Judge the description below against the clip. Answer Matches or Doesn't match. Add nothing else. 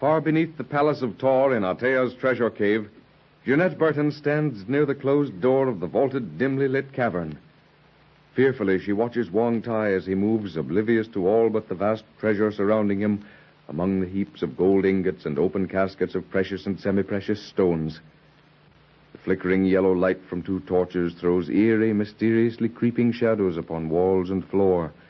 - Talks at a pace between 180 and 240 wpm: Doesn't match